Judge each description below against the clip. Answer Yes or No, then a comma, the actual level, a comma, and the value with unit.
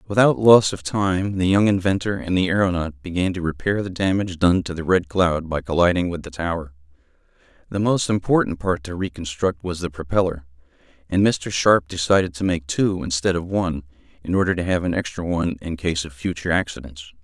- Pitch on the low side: Yes, very low, 90 Hz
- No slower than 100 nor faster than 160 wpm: No, average, 195 wpm